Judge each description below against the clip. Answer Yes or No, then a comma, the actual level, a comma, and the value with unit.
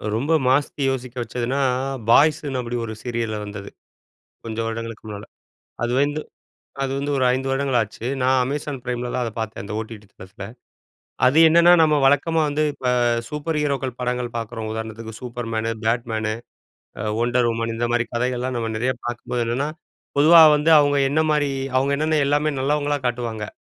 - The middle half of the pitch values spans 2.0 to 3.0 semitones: No, average, 3.9 semitones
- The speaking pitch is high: No, low, 125 Hz